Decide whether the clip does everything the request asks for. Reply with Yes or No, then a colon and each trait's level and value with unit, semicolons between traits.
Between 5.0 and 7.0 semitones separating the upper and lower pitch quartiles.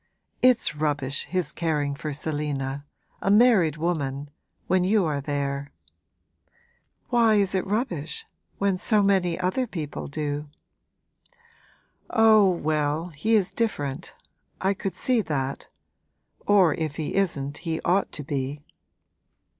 Yes: average, 5.3 semitones